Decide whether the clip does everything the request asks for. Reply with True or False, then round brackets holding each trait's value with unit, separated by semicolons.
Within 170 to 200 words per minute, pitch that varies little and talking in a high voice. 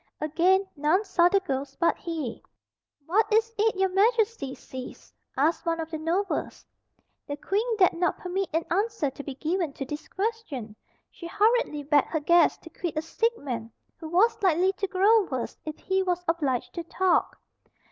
False (175 wpm; 4.6 semitones; 345 Hz)